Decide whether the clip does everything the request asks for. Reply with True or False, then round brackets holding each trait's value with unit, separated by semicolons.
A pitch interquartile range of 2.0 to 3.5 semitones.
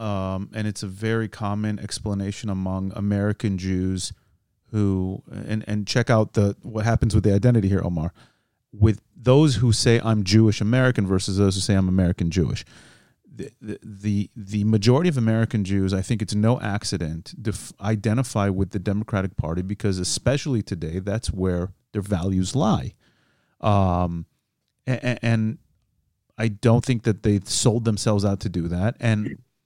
True (2.6 semitones)